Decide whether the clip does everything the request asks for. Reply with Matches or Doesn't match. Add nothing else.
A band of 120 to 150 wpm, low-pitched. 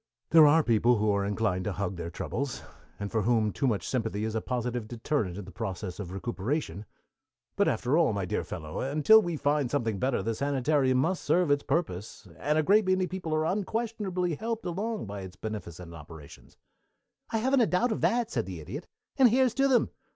Doesn't match